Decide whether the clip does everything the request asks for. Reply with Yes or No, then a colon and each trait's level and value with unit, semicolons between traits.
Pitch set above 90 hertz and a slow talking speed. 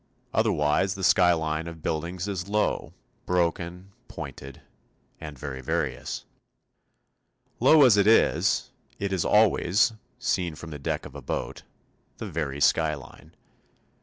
No: very low, 85 Hz; slow, 125 wpm